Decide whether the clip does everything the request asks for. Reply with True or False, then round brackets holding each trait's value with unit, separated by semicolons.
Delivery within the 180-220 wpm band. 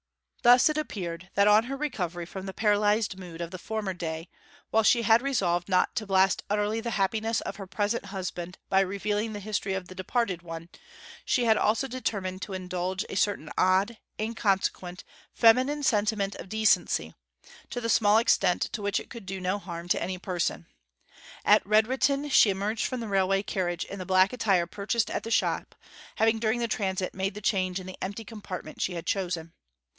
True (190 wpm)